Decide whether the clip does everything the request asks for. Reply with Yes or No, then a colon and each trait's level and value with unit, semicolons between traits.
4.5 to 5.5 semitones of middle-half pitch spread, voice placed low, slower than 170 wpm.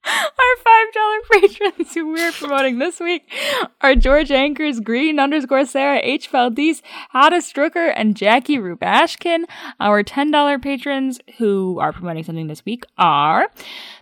No: average, 4.9 semitones; very high, 280 Hz; average, 145 wpm